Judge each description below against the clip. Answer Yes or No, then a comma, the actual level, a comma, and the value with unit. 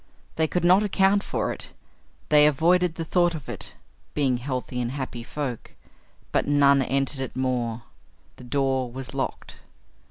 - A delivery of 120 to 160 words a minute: Yes, average, 155 wpm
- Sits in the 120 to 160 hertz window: Yes, medium, 140 Hz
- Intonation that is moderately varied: Yes, average, 4.1 semitones